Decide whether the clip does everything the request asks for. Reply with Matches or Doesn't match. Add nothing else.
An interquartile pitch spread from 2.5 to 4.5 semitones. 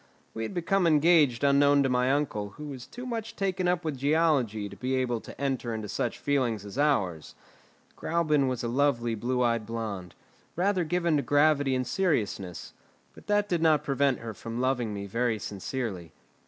Doesn't match